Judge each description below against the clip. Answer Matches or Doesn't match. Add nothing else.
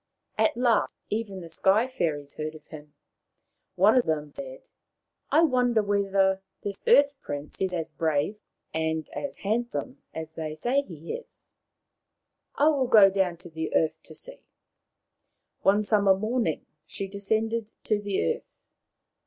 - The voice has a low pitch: Doesn't match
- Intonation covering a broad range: Matches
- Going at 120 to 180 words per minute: Matches